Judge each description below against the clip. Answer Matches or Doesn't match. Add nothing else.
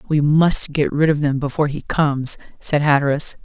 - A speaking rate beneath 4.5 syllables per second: Doesn't match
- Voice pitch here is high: Doesn't match